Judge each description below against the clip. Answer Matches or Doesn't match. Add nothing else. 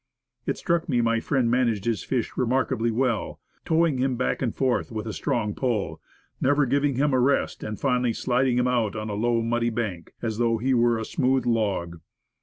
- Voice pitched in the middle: Doesn't match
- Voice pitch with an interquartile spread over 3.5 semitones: Doesn't match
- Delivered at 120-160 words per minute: Doesn't match